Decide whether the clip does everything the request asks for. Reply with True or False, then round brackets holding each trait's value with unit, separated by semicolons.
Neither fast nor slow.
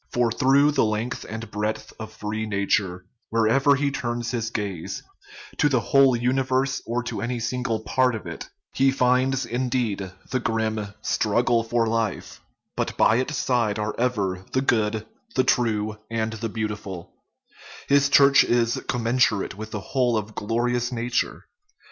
True (165 wpm)